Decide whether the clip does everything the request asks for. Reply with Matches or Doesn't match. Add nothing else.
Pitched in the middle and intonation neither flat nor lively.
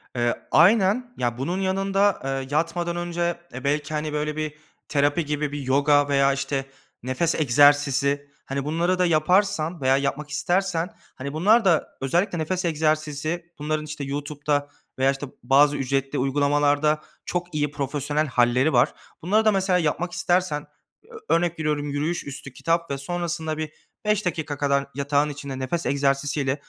Matches